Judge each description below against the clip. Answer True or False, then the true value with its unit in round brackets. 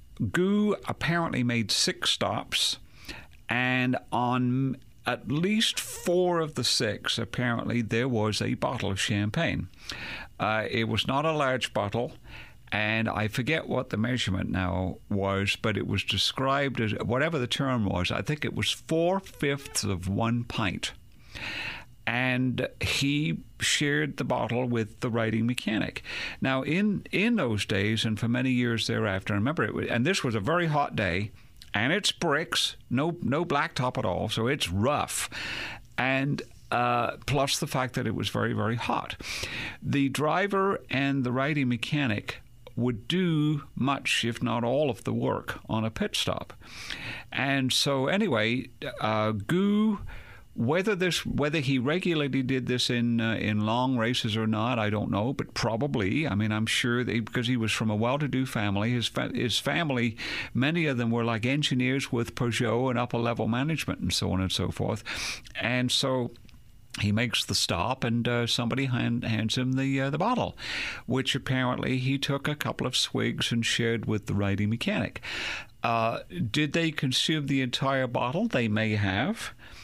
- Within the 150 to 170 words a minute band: True (165 wpm)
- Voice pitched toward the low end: True (120 Hz)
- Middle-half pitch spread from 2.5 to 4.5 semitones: True (3.6 semitones)